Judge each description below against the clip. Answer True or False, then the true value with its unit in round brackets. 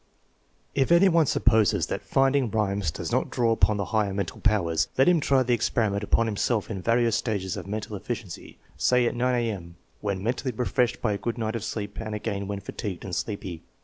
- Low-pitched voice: True (110 Hz)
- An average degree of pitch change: True (3.3 semitones)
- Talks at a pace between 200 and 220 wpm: True (205 wpm)